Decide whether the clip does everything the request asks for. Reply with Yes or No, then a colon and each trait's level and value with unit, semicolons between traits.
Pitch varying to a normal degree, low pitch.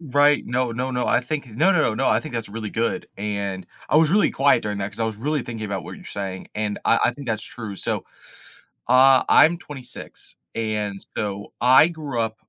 Yes: average, 4.8 semitones; low, 115 Hz